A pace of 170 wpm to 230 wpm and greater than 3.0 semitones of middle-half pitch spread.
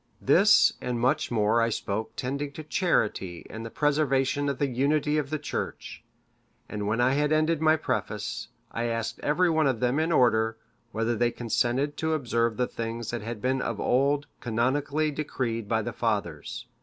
Yes: average, 180 wpm; average, 4.3 semitones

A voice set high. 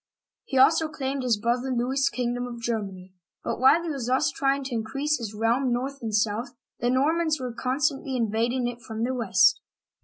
Yes: very high, 250 Hz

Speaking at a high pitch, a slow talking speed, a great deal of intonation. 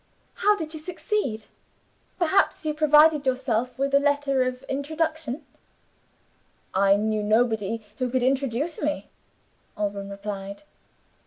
Yes: very high, 265 Hz; slow, 115 wpm; wide, 5.8 semitones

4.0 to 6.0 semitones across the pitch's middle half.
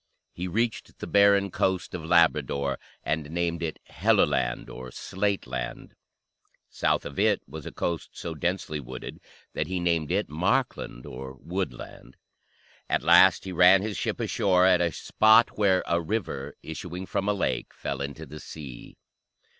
Yes: average, 4.4 semitones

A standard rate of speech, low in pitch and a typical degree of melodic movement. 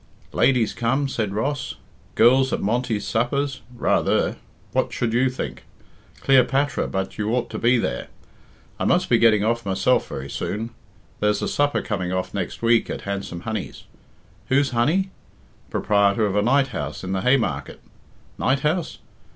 Yes: average, 155 wpm; low, 115 Hz; average, 4.4 semitones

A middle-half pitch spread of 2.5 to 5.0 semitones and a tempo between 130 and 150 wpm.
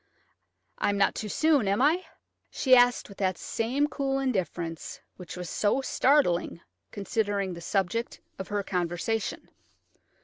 No: wide, 5.6 semitones; average, 140 wpm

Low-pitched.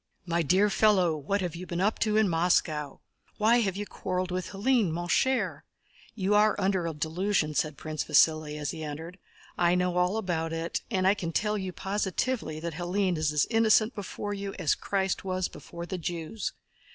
No: medium, 180 Hz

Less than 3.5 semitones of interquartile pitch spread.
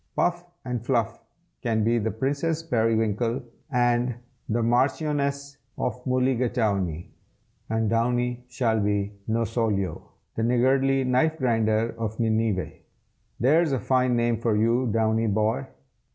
Yes: narrow, 2.5 semitones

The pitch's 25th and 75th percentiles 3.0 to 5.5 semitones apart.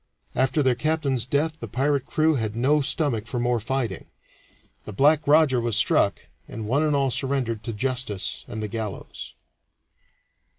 Yes: average, 4.0 semitones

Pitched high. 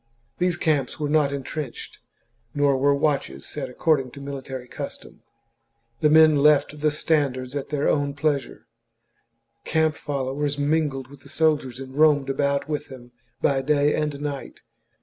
No: medium, 145 Hz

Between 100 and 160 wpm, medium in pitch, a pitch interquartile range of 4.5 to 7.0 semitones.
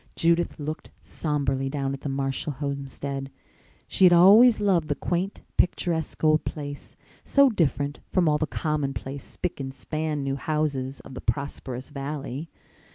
No: average, 150 wpm; medium, 145 Hz; average, 3.1 semitones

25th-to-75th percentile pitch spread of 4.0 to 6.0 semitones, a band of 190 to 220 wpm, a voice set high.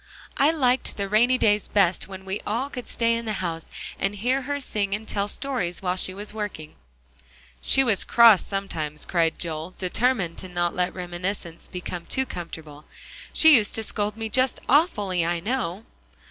No: average, 4.9 semitones; average, 175 wpm; high, 200 Hz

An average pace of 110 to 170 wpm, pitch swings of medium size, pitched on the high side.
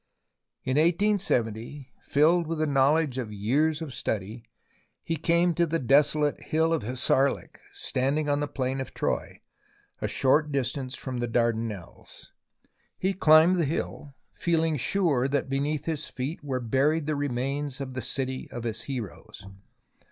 No: average, 150 wpm; average, 3.7 semitones; medium, 140 Hz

